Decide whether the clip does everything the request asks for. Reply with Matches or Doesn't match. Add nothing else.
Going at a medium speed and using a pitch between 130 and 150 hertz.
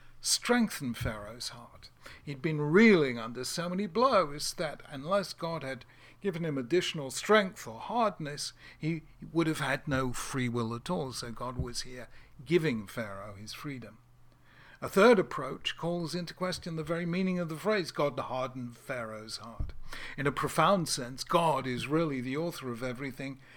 Matches